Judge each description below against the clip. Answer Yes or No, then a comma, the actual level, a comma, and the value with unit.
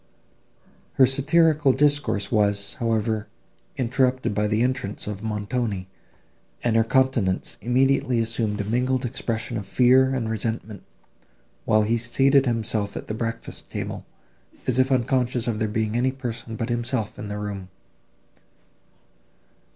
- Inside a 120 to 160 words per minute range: Yes, slow, 135 wpm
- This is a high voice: No, low, 115 Hz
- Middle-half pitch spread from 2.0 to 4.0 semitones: Yes, average, 3.3 semitones